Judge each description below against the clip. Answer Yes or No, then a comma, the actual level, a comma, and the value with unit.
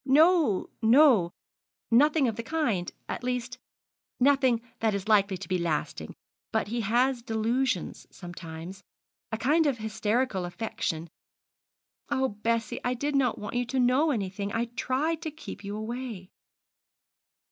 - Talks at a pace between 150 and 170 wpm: No, average, 140 wpm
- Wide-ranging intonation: No, average, 4.4 semitones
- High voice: Yes, high, 230 Hz